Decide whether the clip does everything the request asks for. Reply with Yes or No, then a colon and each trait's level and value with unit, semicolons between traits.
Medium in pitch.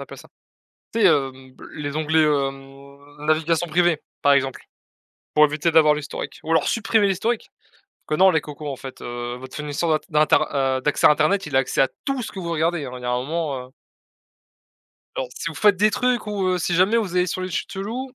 Yes: medium, 155 Hz